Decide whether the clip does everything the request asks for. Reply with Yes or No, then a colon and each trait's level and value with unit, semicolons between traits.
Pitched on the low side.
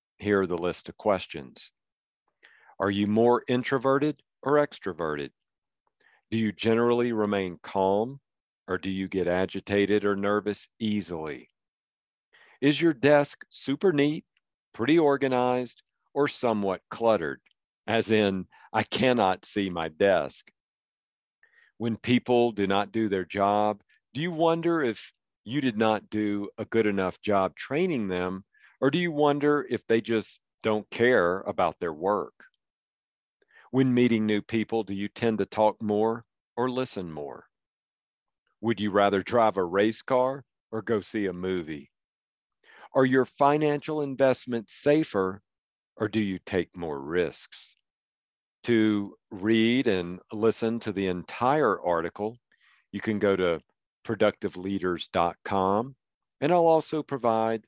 Yes: low, 110 Hz